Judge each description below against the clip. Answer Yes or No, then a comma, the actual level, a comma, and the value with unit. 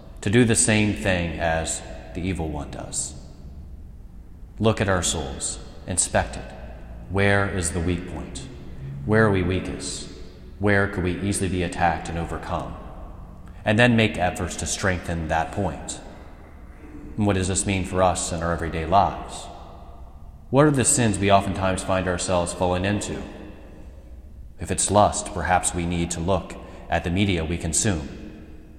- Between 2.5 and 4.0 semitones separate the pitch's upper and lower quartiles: Yes, average, 3.7 semitones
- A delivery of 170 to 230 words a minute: No, average, 155 wpm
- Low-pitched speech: Yes, very low, 90 Hz